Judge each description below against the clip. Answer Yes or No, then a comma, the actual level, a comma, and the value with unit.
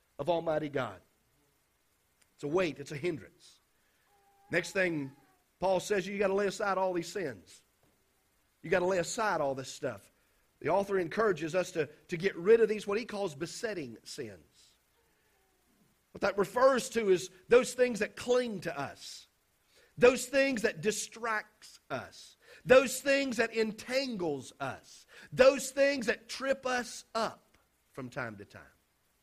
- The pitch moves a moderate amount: No, wide, 6.4 semitones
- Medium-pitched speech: No, high, 200 Hz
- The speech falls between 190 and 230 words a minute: No, average, 155 wpm